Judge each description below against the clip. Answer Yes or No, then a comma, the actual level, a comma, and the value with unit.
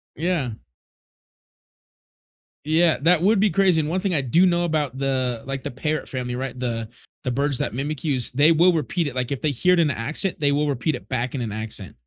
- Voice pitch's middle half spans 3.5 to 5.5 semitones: Yes, average, 4.7 semitones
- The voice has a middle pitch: Yes, medium, 145 Hz